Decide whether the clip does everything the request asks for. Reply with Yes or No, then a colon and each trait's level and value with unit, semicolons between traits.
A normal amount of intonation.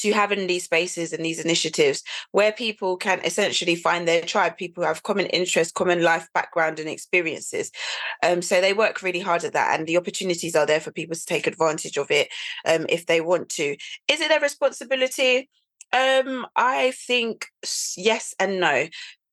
No: wide, 7.4 semitones